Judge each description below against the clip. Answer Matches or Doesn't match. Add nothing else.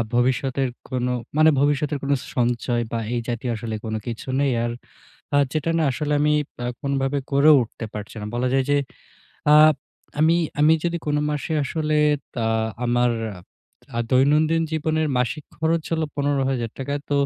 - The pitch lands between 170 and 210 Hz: Doesn't match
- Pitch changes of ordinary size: Matches